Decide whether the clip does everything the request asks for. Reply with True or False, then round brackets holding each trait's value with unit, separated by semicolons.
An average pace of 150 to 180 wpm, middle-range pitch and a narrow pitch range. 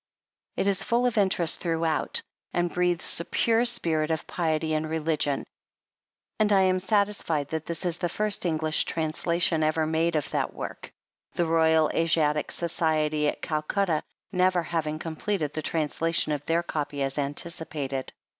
True (155 wpm; 160 Hz; 2.3 semitones)